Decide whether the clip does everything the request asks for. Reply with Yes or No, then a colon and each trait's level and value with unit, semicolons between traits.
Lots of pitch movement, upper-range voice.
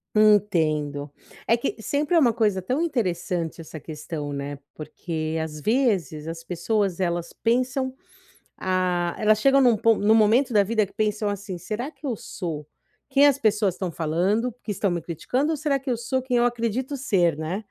Yes: wide, 6.3 semitones; high, 210 Hz